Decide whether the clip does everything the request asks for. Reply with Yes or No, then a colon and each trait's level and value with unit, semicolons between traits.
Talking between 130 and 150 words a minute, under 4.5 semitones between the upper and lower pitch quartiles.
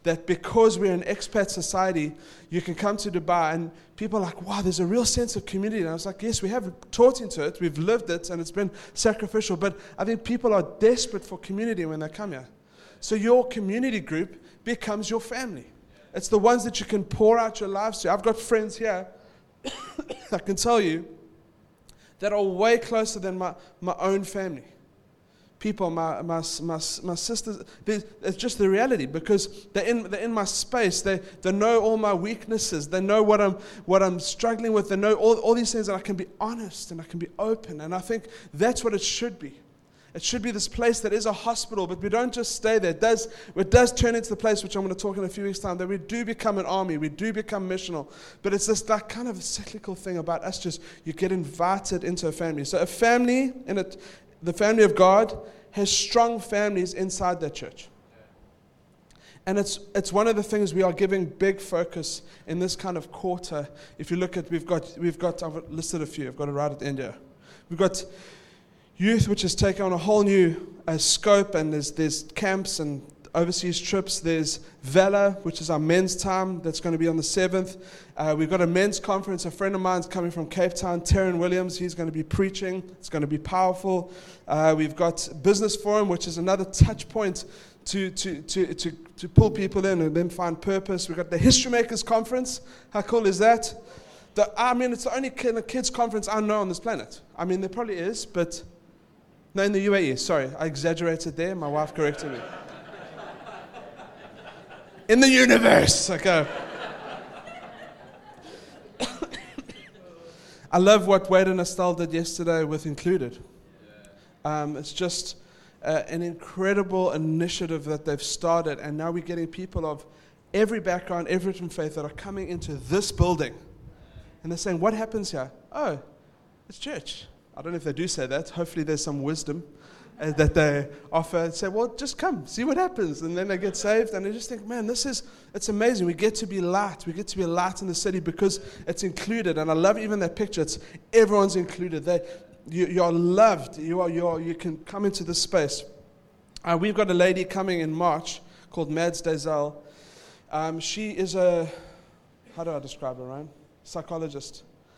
No: average, 200 wpm; average, 3.9 semitones